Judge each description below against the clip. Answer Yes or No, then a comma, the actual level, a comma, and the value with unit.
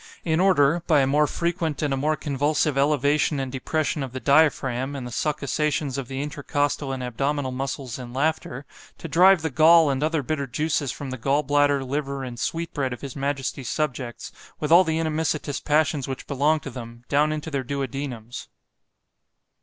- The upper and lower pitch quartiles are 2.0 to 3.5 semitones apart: Yes, narrow, 2.4 semitones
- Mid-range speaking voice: Yes, medium, 145 Hz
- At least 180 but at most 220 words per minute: Yes, average, 185 wpm